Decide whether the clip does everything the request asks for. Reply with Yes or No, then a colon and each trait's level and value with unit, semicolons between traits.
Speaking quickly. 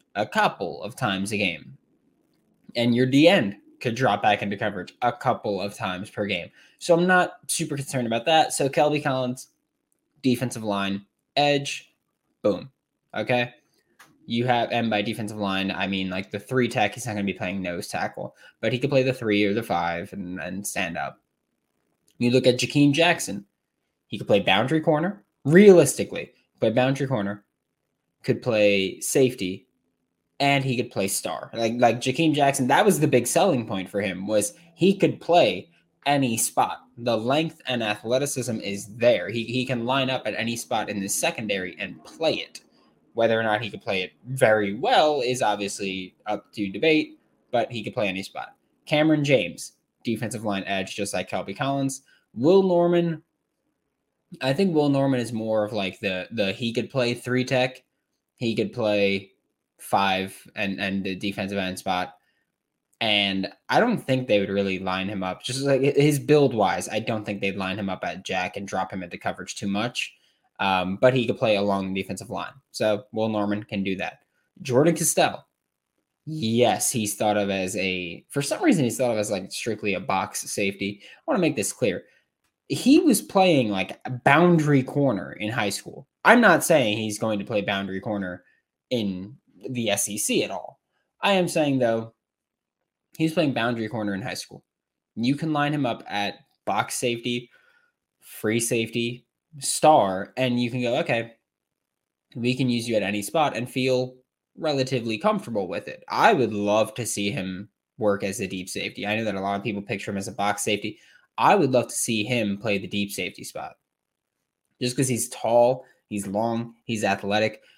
No: average, 185 wpm